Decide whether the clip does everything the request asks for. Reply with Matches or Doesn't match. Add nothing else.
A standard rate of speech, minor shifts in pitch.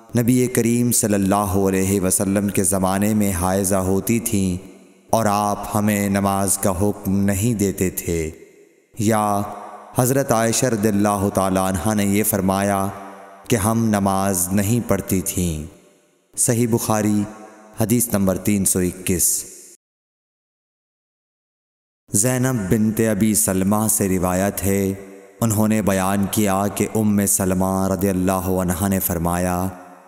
Matches